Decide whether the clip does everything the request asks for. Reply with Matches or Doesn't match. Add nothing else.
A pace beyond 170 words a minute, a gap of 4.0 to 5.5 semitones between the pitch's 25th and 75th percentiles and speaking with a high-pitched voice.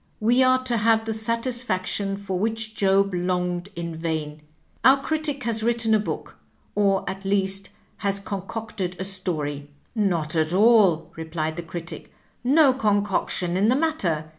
Doesn't match